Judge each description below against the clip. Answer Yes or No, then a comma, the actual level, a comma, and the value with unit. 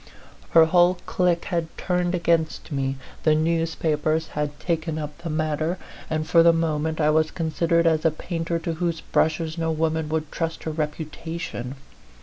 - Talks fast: No, average, 160 wpm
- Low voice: No, medium, 160 Hz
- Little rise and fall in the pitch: Yes, narrow, 1.3 semitones